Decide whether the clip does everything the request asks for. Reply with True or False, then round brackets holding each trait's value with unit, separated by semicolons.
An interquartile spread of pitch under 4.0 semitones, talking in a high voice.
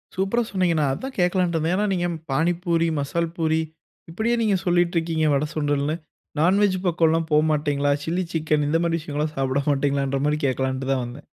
False (3.4 semitones; 160 Hz)